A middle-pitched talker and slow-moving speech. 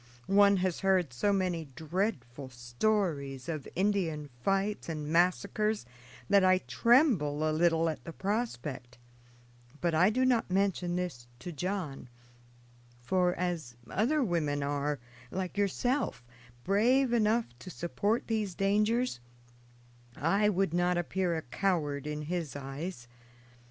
Yes: medium, 180 Hz; slow, 125 wpm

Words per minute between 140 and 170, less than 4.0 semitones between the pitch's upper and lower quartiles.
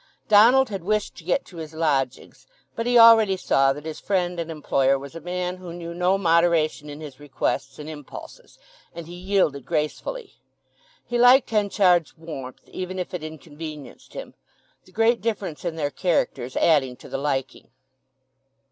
No: average, 165 wpm; average, 4.9 semitones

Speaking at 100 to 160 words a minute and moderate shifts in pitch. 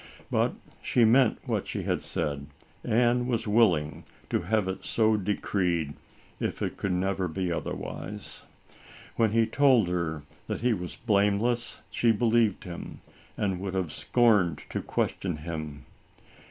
Yes: average, 150 wpm; average, 4.6 semitones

